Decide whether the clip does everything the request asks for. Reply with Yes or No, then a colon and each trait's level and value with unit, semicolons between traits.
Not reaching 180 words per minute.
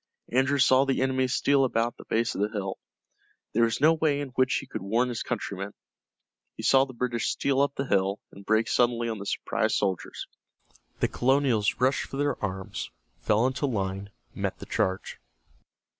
No: average, 185 wpm